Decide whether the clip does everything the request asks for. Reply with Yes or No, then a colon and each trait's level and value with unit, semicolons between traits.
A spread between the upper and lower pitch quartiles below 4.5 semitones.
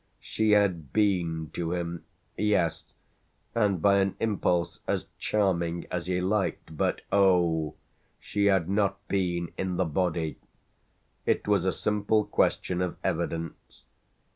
Yes: average, 3.0 semitones